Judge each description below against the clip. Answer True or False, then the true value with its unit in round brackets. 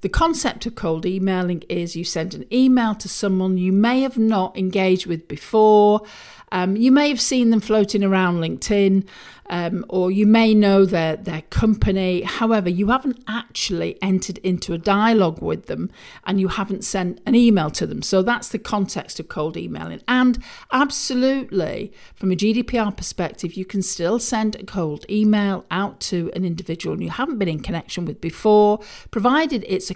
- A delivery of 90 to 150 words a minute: False (175 wpm)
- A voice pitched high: True (200 Hz)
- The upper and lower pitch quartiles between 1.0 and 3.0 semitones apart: False (3.5 semitones)